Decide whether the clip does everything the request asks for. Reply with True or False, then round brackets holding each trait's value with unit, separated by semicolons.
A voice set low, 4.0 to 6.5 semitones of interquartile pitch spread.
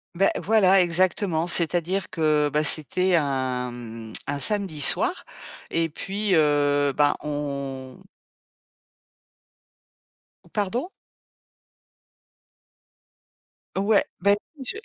False (160 Hz; 5.2 semitones)